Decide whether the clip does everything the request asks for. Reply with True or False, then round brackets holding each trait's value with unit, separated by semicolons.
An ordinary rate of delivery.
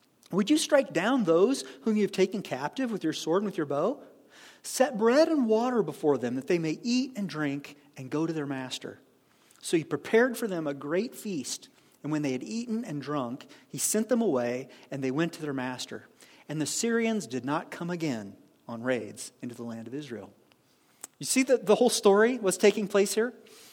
False (210 wpm)